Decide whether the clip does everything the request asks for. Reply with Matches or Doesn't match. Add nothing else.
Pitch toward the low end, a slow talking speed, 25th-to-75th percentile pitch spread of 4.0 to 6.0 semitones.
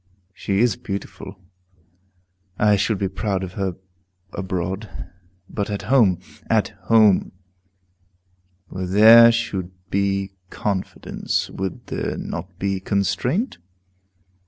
Doesn't match